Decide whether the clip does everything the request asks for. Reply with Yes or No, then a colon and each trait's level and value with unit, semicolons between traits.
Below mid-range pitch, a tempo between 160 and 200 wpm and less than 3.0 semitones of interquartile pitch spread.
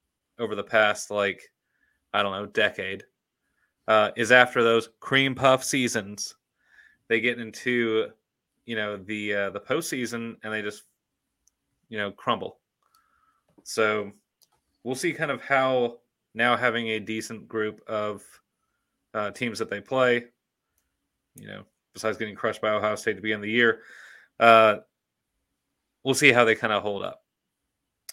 No: low, 110 Hz; average, 145 wpm; narrow, 2.5 semitones